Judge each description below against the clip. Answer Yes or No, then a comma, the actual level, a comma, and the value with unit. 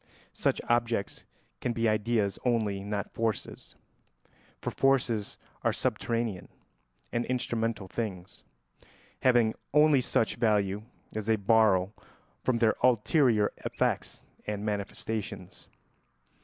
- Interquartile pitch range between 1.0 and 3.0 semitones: Yes, narrow, 2.5 semitones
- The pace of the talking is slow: Yes, slow, 100 wpm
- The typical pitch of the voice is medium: No, low, 110 Hz